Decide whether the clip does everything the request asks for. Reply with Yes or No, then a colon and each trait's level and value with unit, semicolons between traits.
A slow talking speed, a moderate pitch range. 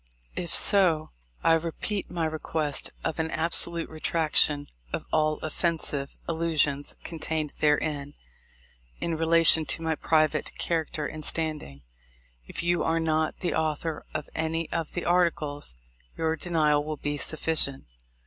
No: slow, 130 wpm; narrow, 1.5 semitones